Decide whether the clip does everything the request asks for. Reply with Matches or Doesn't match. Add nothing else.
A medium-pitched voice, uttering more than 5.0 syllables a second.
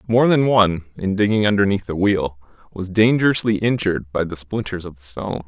Doesn't match